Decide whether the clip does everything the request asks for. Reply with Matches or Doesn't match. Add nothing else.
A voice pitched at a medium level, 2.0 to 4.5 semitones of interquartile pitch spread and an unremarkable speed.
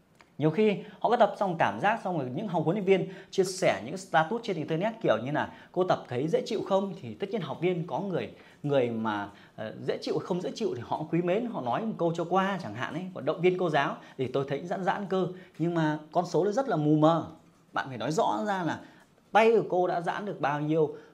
Doesn't match